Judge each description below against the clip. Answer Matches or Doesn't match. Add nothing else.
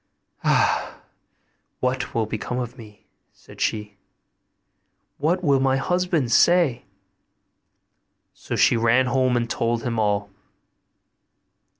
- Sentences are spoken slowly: Matches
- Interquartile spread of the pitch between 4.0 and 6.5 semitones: Doesn't match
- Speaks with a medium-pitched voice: Doesn't match